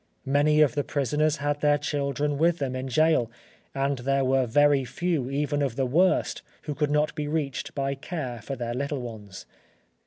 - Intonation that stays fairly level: Yes, narrow, 2.2 semitones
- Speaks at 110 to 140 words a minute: No, average, 185 wpm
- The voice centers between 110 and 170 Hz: Yes, medium, 140 Hz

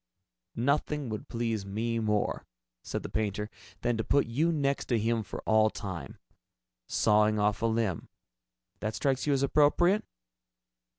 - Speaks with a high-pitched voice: No, low, 115 Hz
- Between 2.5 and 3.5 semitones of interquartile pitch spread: No, average, 4.5 semitones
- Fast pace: No, average, 150 wpm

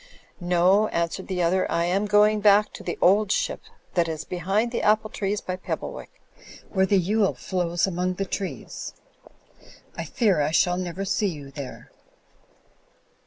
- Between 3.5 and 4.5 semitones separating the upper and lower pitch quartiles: No, average, 3.0 semitones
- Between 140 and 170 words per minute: Yes, average, 165 wpm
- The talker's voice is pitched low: No, medium, 185 Hz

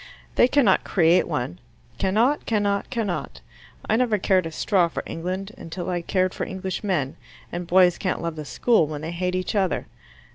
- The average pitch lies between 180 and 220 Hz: Yes, medium, 185 Hz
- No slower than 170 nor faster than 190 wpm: Yes, average, 175 wpm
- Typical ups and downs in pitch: Yes, average, 3.1 semitones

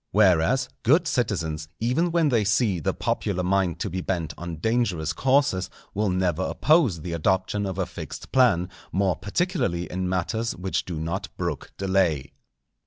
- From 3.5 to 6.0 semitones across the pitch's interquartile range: Yes, average, 5.0 semitones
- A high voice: No, very low, 95 Hz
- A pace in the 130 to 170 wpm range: Yes, average, 160 wpm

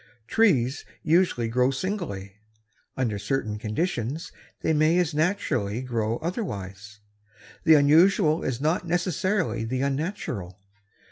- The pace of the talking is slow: Yes, slow, 110 wpm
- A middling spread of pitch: No, wide, 7.4 semitones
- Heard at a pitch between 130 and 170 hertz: Yes, medium, 140 Hz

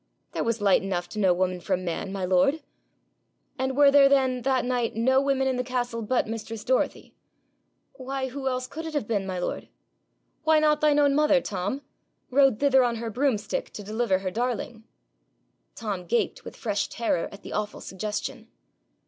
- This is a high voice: Yes, high, 240 Hz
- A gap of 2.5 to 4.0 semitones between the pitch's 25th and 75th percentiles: No, average, 4.7 semitones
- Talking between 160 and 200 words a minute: Yes, average, 180 wpm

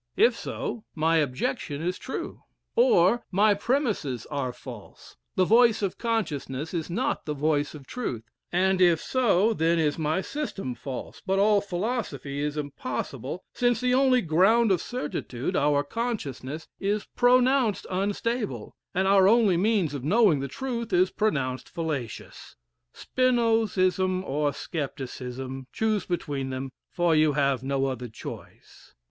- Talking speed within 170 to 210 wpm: No, average, 140 wpm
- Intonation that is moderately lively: No, wide, 7.7 semitones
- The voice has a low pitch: No, medium, 175 Hz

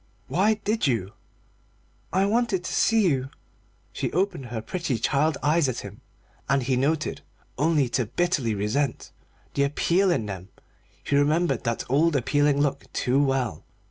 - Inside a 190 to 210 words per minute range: No, average, 150 wpm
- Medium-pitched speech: Yes, medium, 145 Hz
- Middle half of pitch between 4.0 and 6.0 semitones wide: Yes, average, 5.2 semitones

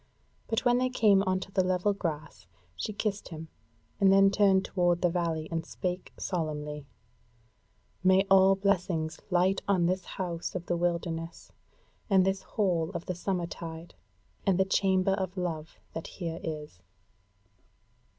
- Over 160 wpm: No, average, 150 wpm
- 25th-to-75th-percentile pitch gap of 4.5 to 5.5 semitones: No, average, 2.7 semitones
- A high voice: No, medium, 180 Hz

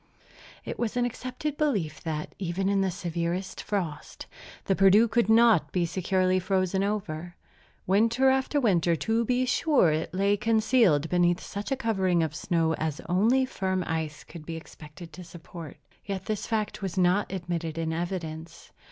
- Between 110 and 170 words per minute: Yes, average, 160 wpm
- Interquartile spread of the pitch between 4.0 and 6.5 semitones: Yes, average, 4.5 semitones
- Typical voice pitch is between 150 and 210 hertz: Yes, medium, 185 Hz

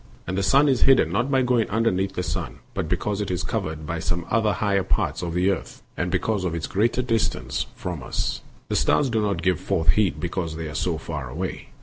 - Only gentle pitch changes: No, average, 4.6 semitones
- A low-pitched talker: Yes, very low, 95 Hz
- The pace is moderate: No, fast, 235 wpm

